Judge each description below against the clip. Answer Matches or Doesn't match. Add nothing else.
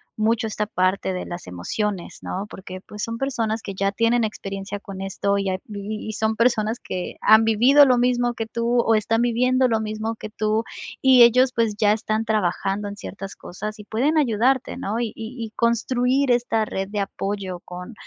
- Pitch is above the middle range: Matches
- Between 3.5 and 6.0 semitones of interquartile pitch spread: Doesn't match